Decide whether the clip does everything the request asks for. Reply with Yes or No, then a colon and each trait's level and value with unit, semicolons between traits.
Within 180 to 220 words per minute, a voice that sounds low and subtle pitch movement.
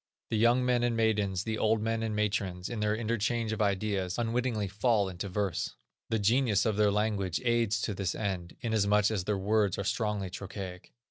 Yes: average, 190 wpm; low, 105 Hz; narrow, 2.3 semitones